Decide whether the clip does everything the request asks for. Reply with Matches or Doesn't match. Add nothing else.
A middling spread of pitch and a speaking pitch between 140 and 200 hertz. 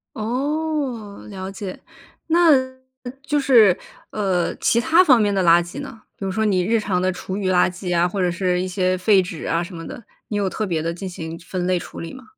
Matches